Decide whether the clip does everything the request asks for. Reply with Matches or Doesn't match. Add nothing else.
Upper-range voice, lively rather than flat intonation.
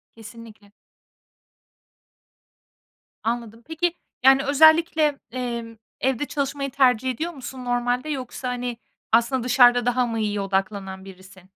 Doesn't match